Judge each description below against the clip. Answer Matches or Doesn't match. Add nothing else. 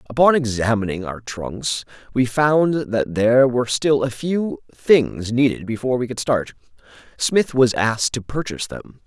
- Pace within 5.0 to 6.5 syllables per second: Doesn't match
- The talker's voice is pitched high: Doesn't match